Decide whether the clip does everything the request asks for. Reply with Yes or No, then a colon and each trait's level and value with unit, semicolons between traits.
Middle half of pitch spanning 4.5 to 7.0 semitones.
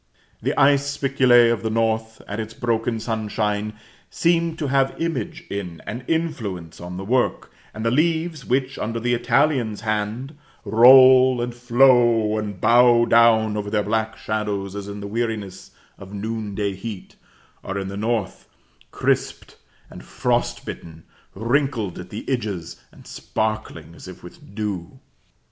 No: average, 3.5 semitones